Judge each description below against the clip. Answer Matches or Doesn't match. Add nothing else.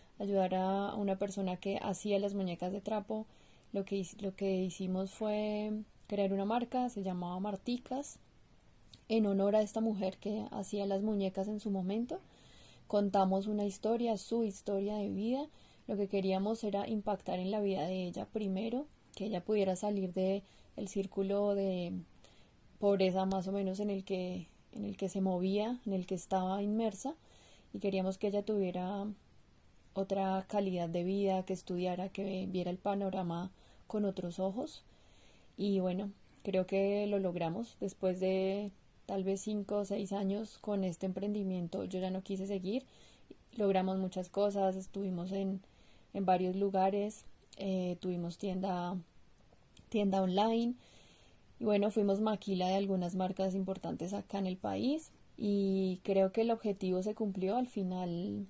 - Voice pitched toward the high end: Matches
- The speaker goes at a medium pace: Matches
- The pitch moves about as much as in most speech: Doesn't match